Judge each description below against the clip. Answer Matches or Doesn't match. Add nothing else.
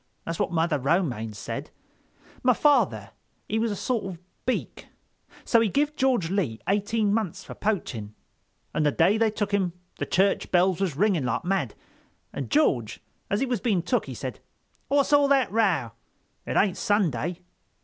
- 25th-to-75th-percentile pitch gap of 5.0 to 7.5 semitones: Matches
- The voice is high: Matches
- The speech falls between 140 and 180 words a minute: Matches